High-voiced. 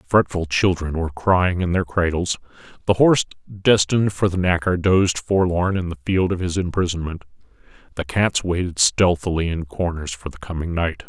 No: very low, 90 Hz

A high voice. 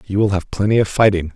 No: low, 100 Hz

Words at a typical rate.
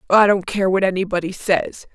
Yes: average, 185 wpm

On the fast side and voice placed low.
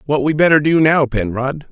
No: fast, 210 wpm; medium, 145 Hz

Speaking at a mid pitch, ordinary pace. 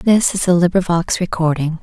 Yes: medium, 175 Hz; average, 165 wpm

